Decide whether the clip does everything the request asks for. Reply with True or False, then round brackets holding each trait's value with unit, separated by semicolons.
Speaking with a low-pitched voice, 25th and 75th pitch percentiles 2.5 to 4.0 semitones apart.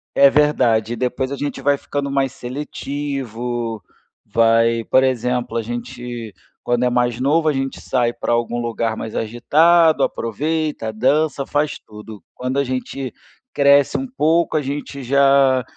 True (130 Hz; 3.2 semitones)